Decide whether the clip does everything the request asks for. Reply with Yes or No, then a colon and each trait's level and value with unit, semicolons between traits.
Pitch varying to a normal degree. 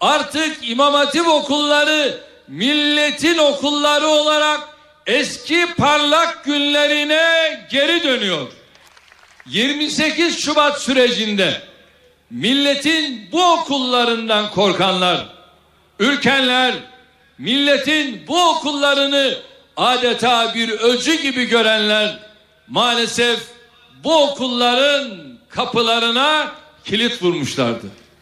Yes: average, 4.2 semitones